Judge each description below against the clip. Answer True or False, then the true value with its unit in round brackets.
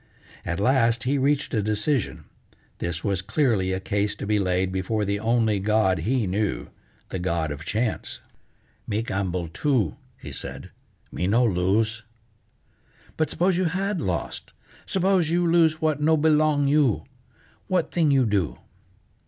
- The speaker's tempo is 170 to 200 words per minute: False (150 wpm)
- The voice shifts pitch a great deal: True (7.5 semitones)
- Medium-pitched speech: False (110 Hz)